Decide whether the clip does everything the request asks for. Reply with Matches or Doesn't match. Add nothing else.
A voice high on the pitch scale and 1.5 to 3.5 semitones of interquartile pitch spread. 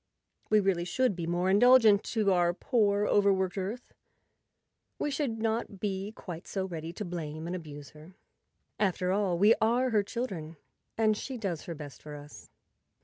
Doesn't match